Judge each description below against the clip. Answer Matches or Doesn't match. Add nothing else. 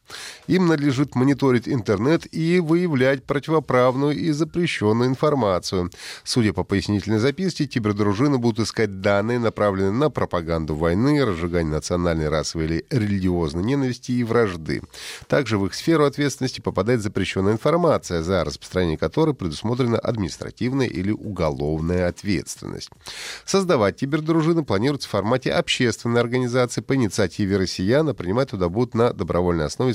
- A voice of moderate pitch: Doesn't match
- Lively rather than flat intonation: Matches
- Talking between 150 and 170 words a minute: Doesn't match